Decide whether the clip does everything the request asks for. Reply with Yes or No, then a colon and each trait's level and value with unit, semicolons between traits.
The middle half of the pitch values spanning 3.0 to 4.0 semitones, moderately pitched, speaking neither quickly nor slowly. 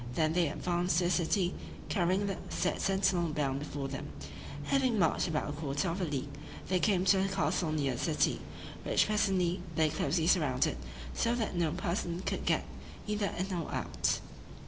Yes: average, 3.7 semitones; medium, 175 Hz; average, 180 wpm